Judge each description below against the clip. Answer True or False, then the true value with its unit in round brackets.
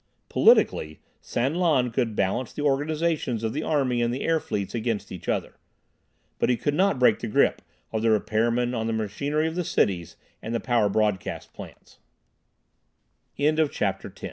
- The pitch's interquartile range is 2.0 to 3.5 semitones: False (5.0 semitones)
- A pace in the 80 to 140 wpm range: False (160 wpm)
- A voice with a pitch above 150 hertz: False (120 Hz)